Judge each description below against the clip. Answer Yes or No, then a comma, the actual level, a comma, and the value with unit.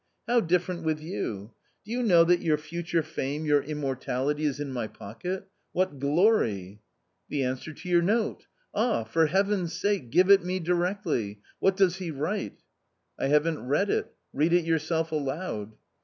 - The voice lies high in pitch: No, medium, 160 Hz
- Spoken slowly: No, average, 185 wpm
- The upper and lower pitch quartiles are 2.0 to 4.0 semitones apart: No, average, 4.6 semitones